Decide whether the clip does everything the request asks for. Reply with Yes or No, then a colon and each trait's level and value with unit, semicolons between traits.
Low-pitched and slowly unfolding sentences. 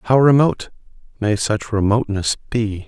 Yes: low, 110 Hz; slow, 125 wpm